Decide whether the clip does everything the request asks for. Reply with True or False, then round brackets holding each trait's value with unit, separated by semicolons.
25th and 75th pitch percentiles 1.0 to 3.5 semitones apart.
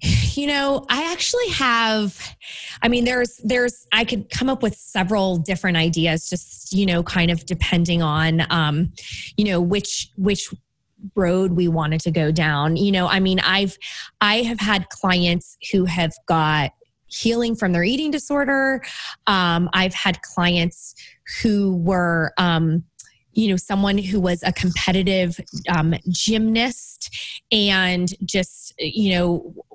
False (3.9 semitones)